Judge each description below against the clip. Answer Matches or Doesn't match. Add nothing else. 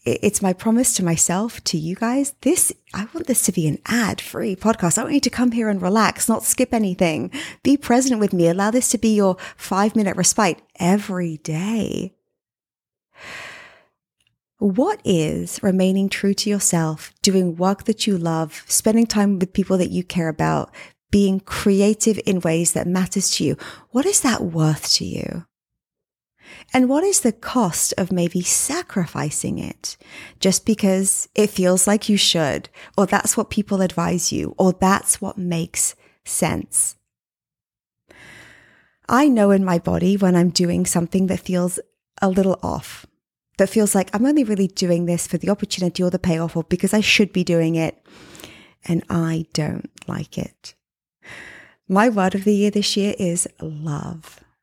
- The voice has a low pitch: Doesn't match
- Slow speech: Doesn't match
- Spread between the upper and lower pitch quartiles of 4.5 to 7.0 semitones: Doesn't match